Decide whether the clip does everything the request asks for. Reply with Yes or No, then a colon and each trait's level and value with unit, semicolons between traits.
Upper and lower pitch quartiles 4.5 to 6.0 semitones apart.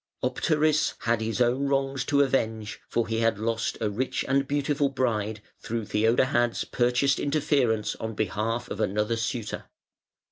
No: average, 3.6 semitones